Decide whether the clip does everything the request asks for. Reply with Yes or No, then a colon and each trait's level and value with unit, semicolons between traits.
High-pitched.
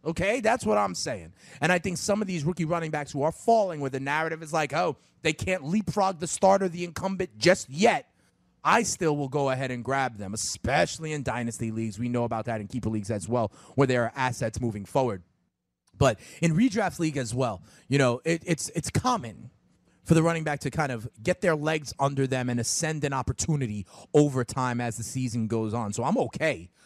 No: medium, 140 Hz